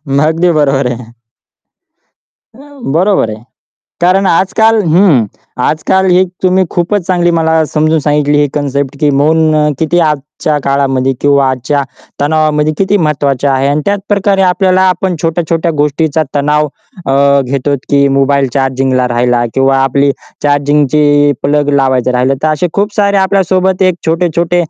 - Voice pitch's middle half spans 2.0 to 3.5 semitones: No, average, 4.1 semitones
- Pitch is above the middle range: No, medium, 150 Hz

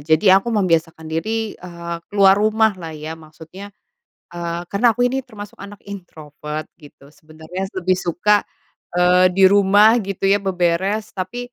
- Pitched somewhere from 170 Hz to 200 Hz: Yes, medium, 185 Hz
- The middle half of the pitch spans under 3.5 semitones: No, average, 4.0 semitones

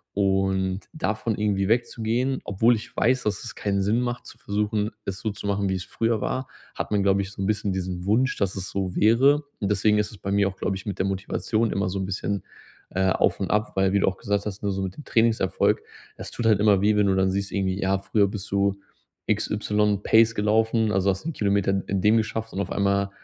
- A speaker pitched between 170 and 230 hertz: No, low, 100 Hz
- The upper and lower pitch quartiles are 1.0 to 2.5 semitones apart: Yes, narrow, 2.0 semitones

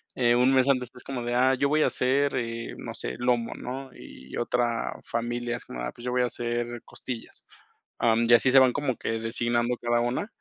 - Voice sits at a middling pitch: No, low, 120 Hz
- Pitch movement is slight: Yes, narrow, 1.5 semitones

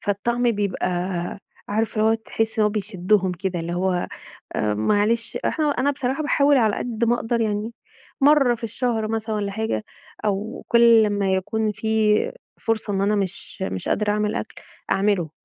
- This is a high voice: Yes, high, 215 Hz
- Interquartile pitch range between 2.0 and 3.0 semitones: Yes, narrow, 2.5 semitones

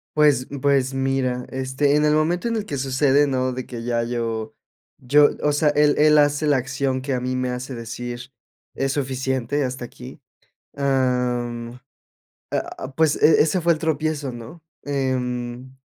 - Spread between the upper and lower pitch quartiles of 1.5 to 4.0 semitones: Yes, average, 2.7 semitones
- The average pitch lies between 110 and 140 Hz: Yes, low, 135 Hz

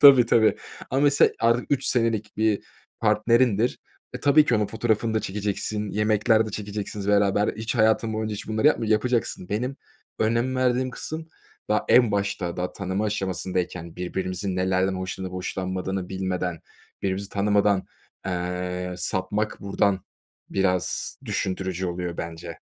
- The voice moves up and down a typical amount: Yes, average, 3.1 semitones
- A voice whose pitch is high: No, low, 105 Hz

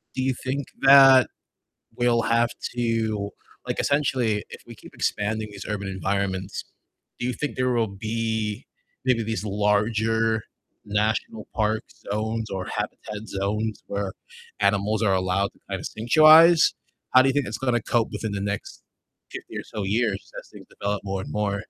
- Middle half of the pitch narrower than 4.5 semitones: Yes, average, 2.8 semitones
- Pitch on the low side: Yes, low, 110 Hz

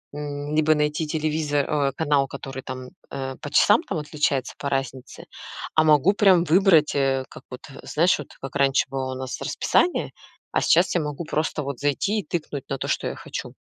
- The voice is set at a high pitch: No, medium, 145 Hz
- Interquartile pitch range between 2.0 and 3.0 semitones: Yes, narrow, 2.5 semitones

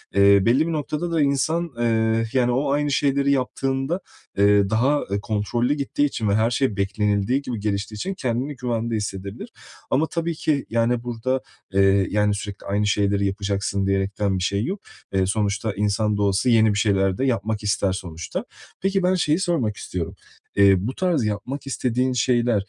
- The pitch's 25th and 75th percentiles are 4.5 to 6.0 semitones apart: Yes, average, 5.1 semitones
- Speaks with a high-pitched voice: No, low, 115 Hz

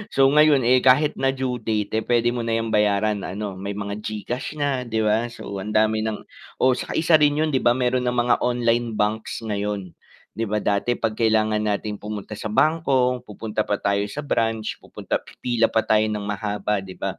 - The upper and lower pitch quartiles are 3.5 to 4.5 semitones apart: No, average, 2.9 semitones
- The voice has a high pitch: No, low, 110 Hz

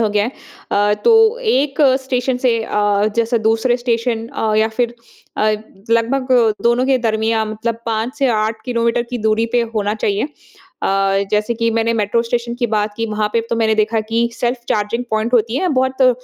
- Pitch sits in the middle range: No, high, 230 Hz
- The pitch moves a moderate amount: No, narrow, 2.0 semitones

